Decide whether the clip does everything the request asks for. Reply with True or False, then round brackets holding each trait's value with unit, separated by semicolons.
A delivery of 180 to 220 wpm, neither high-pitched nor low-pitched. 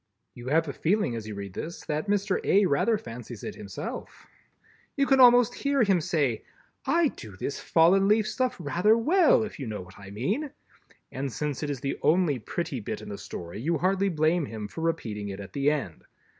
True (205 wpm; 155 Hz)